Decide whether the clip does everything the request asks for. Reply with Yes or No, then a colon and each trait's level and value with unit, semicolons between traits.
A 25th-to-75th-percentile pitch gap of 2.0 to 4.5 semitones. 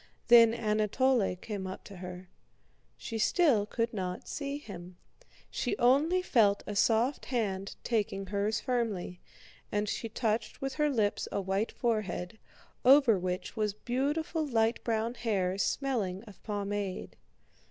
Yes: average, 3.8 semitones